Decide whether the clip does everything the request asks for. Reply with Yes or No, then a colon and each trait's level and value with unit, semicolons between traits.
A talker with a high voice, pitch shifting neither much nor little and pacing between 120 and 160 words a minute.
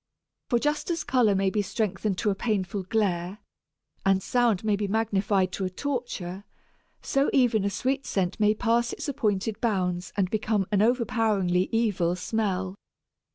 Yes: high, 210 Hz; average, 3.5 semitones; average, 155 wpm